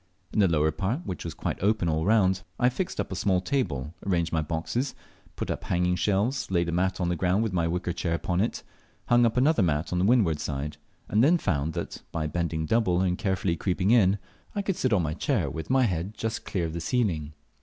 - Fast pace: Yes, fast, 230 wpm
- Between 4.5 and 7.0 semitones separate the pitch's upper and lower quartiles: Yes, average, 4.9 semitones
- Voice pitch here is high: No, very low, 90 Hz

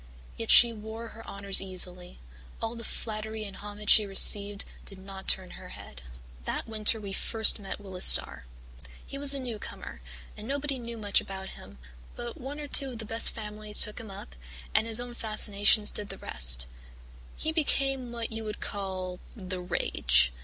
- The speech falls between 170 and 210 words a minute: Yes, average, 180 wpm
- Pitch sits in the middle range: No, high, 210 Hz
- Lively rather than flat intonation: No, average, 3.0 semitones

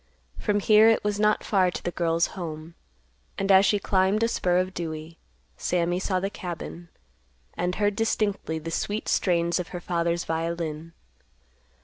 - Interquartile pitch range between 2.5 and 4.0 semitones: Yes, average, 3.1 semitones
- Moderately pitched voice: Yes, medium, 180 Hz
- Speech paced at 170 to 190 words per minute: No, average, 160 wpm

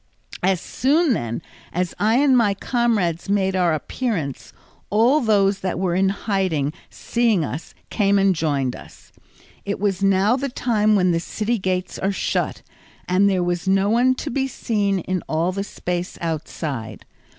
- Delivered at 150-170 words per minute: Yes, average, 160 wpm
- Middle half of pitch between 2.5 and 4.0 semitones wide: Yes, average, 3.7 semitones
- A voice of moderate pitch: No, high, 195 Hz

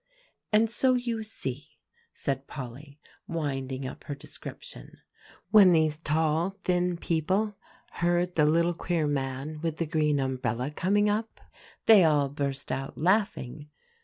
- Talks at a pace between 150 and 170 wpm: No, slow, 135 wpm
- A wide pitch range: No, average, 4.5 semitones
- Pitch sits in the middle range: Yes, medium, 155 Hz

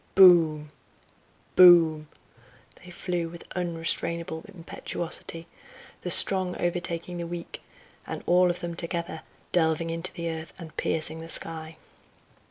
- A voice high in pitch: No, medium, 170 Hz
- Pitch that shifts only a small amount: Yes, narrow, 1.4 semitones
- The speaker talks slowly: Yes, slow, 120 wpm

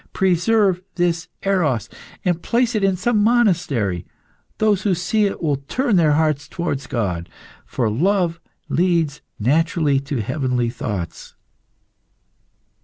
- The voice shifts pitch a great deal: Yes, wide, 6.3 semitones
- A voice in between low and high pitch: Yes, medium, 165 Hz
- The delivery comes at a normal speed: No, slow, 120 wpm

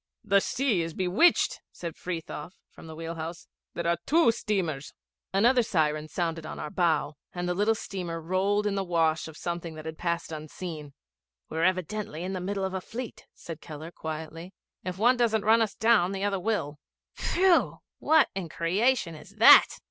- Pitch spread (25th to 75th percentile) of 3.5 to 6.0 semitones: Yes, average, 4.1 semitones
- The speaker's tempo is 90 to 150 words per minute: No, average, 180 wpm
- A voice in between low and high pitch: Yes, medium, 180 Hz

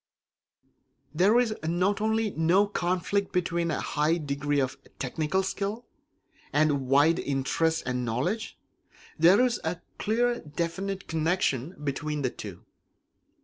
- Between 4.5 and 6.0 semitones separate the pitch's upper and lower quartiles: Yes, average, 5.1 semitones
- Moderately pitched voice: Yes, medium, 170 Hz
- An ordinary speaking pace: No, slow, 125 wpm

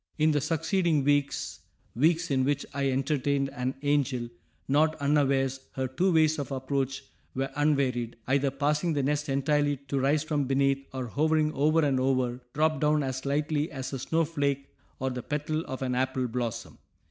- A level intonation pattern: Yes, narrow, 2.3 semitones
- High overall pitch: No, medium, 140 Hz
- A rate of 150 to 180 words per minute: Yes, average, 170 wpm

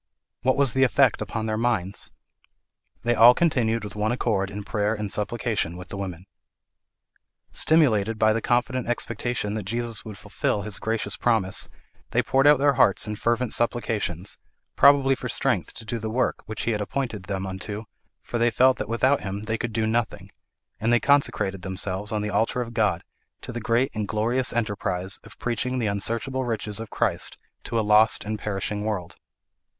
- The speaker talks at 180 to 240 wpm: Yes, average, 185 wpm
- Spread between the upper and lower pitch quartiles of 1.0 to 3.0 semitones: Yes, average, 2.7 semitones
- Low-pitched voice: Yes, low, 110 Hz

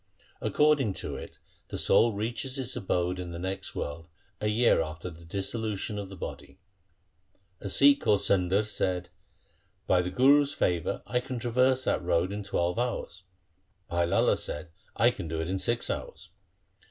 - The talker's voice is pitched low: Yes, low, 100 Hz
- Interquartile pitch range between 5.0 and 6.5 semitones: Yes, average, 5.3 semitones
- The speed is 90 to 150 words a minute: No, average, 175 wpm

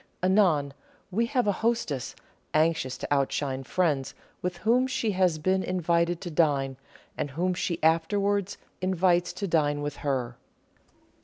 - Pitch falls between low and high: Yes, medium, 175 Hz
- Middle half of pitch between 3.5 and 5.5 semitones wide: Yes, average, 4.5 semitones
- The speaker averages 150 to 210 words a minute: No, average, 140 wpm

